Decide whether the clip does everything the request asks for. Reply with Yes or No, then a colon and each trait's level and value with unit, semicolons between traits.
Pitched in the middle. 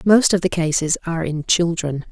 Yes: medium, 170 Hz